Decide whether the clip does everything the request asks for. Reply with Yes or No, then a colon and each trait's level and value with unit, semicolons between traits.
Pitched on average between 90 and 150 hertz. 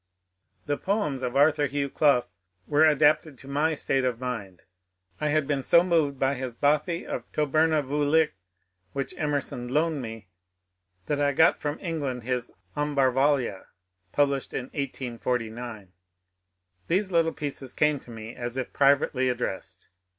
Yes: medium, 140 Hz